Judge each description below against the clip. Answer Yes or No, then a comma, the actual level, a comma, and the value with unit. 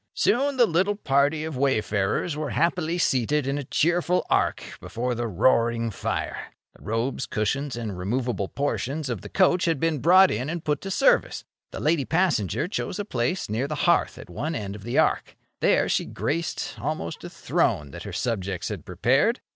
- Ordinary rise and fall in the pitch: No, wide, 6.5 semitones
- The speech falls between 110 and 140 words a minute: No, average, 185 wpm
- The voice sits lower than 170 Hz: Yes, medium, 140 Hz